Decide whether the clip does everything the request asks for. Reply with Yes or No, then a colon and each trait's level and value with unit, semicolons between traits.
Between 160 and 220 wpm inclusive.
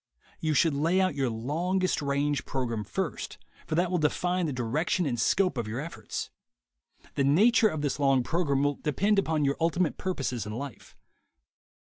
Yes: average, 170 wpm